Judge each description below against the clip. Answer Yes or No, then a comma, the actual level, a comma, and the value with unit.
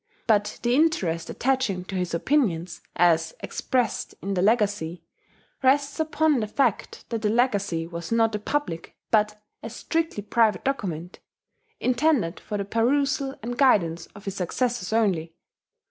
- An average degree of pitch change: No, wide, 6.3 semitones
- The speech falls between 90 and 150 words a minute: Yes, average, 145 wpm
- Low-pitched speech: No, high, 215 Hz